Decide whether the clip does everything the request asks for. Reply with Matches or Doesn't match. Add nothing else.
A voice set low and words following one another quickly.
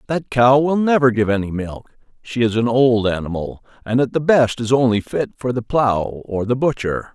Matches